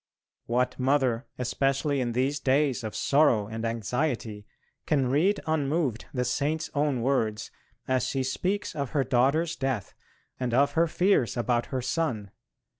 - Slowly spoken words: No, average, 145 wpm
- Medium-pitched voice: No, low, 130 Hz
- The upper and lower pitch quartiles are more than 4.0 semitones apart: No, average, 3.4 semitones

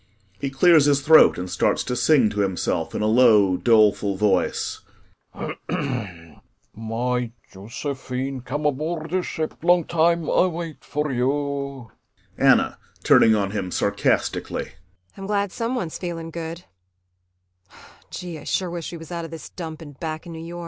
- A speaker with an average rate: No, slow, 95 wpm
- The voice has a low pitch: Yes, low, 130 Hz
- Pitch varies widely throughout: Yes, wide, 5.8 semitones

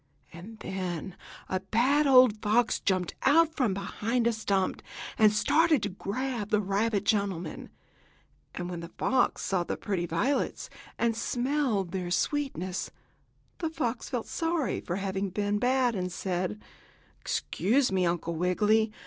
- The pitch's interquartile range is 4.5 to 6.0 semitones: Yes, average, 5.0 semitones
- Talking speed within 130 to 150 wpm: Yes, average, 140 wpm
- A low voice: No, high, 210 Hz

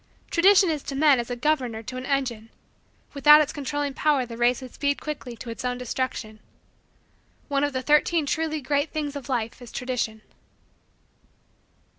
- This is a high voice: Yes, very high, 275 Hz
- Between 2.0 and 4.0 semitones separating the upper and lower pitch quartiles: Yes, average, 3.3 semitones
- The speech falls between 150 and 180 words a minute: Yes, average, 170 wpm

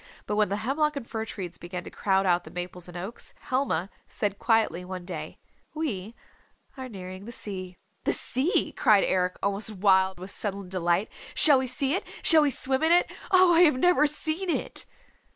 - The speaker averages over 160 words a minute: Yes, average, 190 wpm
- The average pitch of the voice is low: No, high, 210 Hz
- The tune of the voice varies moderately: No, wide, 6.8 semitones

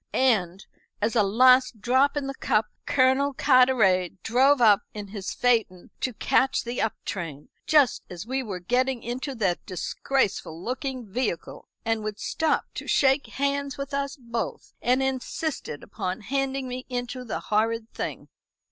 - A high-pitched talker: Yes, high, 245 Hz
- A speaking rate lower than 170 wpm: Yes, average, 155 wpm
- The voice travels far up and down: No, average, 4.0 semitones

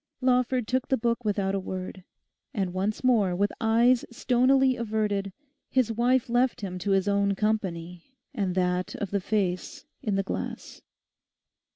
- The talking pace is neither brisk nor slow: Yes, average, 155 wpm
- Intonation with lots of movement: No, average, 4.0 semitones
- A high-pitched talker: Yes, high, 210 Hz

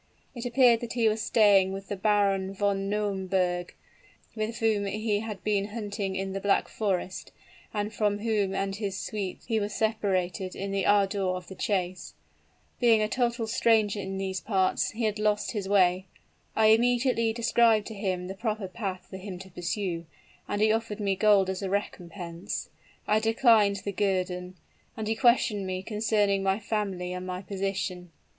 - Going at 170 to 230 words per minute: Yes, average, 175 wpm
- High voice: Yes, high, 200 Hz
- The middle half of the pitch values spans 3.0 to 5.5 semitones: No, narrow, 2.4 semitones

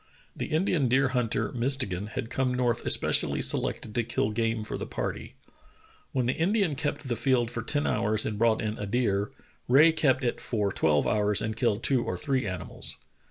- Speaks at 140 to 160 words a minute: No, average, 190 wpm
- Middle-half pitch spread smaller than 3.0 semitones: No, average, 3.8 semitones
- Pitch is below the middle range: Yes, low, 120 Hz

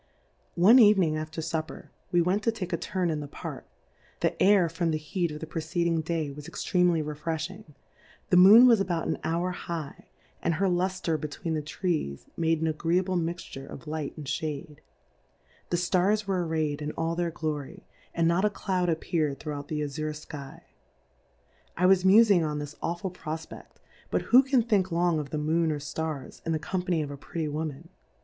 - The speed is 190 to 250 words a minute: Yes, average, 200 wpm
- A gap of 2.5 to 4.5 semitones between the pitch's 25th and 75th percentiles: Yes, average, 3.0 semitones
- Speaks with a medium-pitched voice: Yes, medium, 165 Hz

